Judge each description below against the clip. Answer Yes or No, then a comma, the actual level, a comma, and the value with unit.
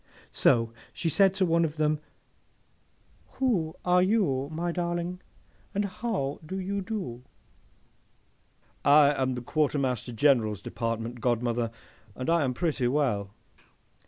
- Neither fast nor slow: No, slow, 120 wpm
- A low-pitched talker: No, medium, 150 Hz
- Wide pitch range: Yes, wide, 6.4 semitones